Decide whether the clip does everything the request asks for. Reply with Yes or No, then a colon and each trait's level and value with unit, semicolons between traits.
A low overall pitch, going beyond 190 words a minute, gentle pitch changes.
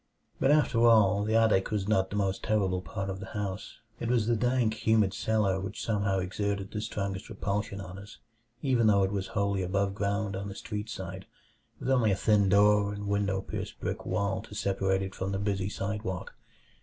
Yes: low, 100 Hz; average, 200 wpm; narrow, 1.8 semitones